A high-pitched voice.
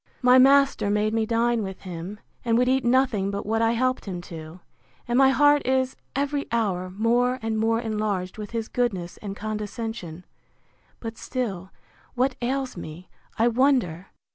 Yes: high, 225 Hz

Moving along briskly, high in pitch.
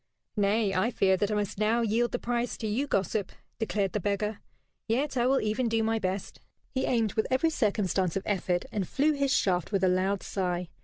Yes: fast, 210 wpm; high, 210 Hz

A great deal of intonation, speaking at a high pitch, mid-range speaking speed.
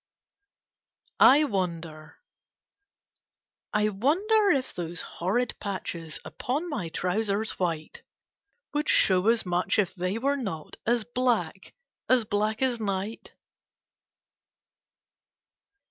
No: wide, 5.7 semitones; high, 210 Hz; slow, 100 wpm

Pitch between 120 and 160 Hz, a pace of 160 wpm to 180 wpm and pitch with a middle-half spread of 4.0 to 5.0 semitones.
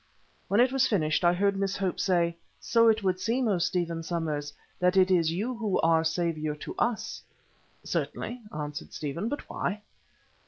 No: medium, 185 Hz; average, 170 wpm; average, 4.6 semitones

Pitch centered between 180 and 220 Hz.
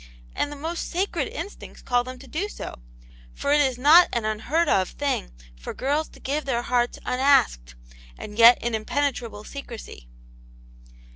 No: very high, 260 Hz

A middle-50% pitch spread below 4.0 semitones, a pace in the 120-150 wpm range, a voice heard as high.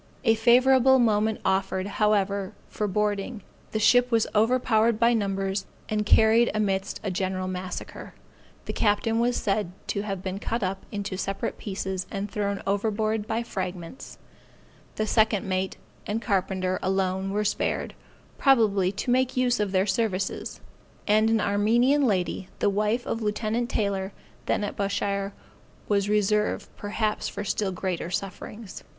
Yes: narrow, 2.5 semitones; average, 145 wpm; high, 205 Hz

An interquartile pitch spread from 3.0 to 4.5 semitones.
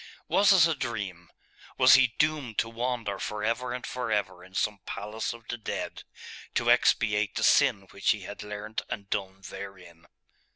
Yes: average, 3.6 semitones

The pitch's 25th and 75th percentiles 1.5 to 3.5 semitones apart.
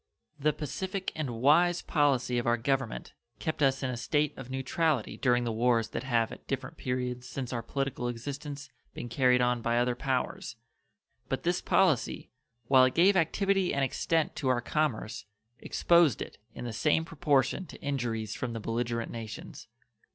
No: average, 3.9 semitones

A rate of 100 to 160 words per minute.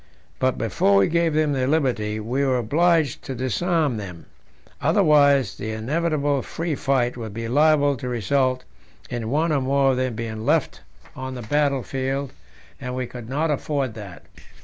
No: average, 170 wpm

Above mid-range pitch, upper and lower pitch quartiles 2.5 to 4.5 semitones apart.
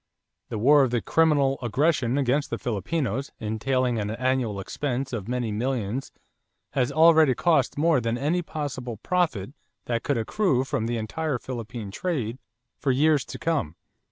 No: low, 130 Hz; average, 4.2 semitones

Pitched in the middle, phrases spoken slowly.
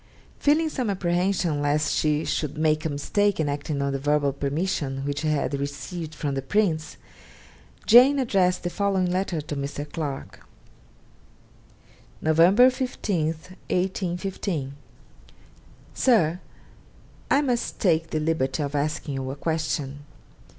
Yes: medium, 160 Hz; slow, 130 wpm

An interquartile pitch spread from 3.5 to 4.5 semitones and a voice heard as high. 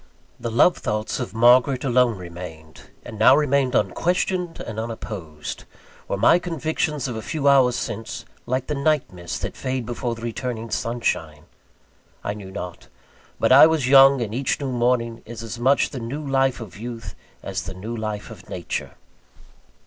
No: average, 3.8 semitones; low, 120 Hz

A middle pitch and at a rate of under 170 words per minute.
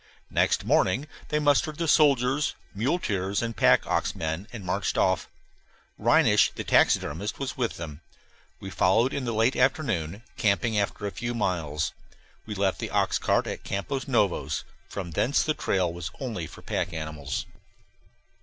No: low, 105 Hz; average, 155 wpm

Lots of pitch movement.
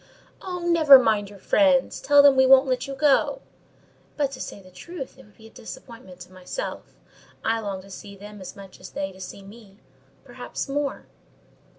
Yes: wide, 6.0 semitones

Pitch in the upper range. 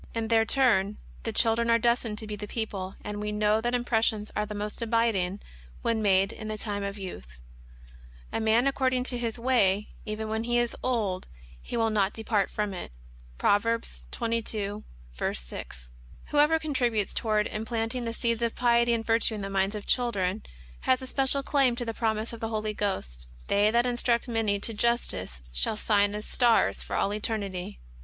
Yes: high, 220 Hz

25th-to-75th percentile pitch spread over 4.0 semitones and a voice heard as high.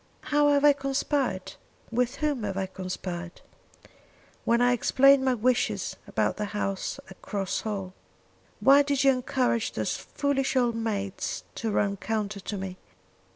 Yes: wide, 5.4 semitones; high, 230 Hz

